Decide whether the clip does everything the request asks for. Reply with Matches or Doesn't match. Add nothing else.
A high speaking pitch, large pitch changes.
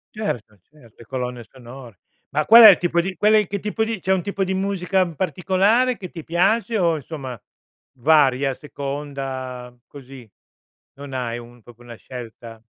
Doesn't match